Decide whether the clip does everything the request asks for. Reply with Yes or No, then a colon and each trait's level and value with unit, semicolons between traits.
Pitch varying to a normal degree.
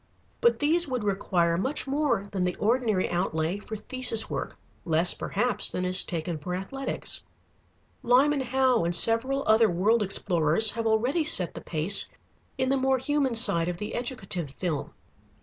No: wide, 6.5 semitones